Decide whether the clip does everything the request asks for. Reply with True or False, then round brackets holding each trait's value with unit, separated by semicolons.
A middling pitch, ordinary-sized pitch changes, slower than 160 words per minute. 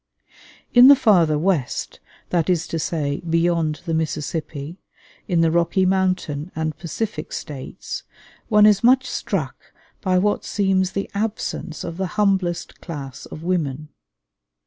True (175 Hz; 3.6 semitones; 135 wpm)